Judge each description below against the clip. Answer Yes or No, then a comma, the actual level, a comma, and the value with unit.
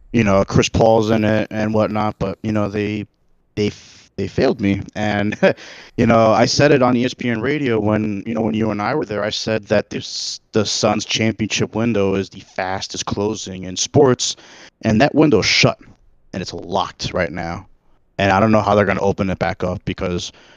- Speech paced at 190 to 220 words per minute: Yes, fast, 205 wpm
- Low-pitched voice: Yes, low, 105 Hz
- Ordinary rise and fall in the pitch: No, narrow, 2.3 semitones